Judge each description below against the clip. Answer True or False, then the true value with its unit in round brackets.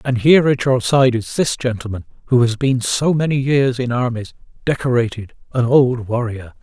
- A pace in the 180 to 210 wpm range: False (170 wpm)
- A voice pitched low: True (125 Hz)